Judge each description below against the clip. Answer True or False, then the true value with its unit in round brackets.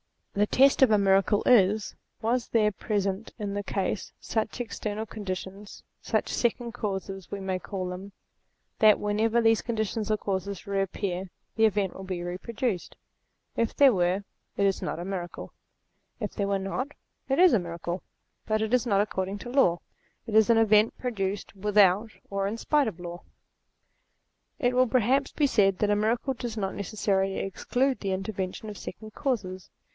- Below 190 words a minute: True (175 wpm)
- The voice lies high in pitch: True (205 Hz)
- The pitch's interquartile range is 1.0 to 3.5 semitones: True (2.8 semitones)